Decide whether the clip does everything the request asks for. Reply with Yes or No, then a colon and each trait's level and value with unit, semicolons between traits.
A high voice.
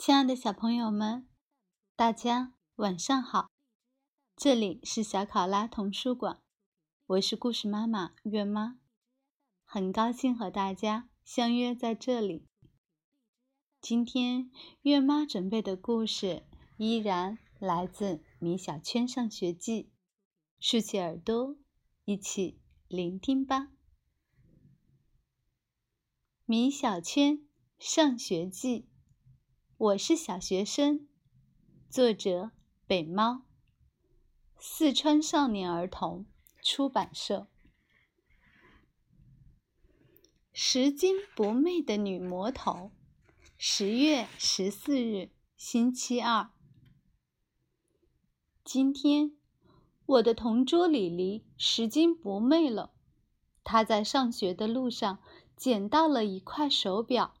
Yes: high, 230 Hz